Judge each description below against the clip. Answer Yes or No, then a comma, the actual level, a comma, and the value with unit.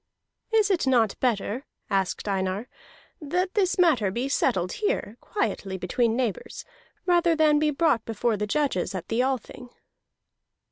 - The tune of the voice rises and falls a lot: Yes, wide, 7.8 semitones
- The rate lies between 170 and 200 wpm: No, average, 140 wpm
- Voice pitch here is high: Yes, very high, 250 Hz